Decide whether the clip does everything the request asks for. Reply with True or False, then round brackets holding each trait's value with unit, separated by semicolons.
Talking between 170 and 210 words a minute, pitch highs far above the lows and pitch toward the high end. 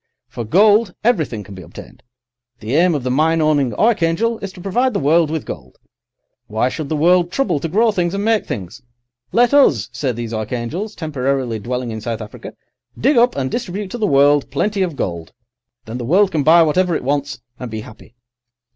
False (200 wpm; 8.1 semitones; 155 Hz)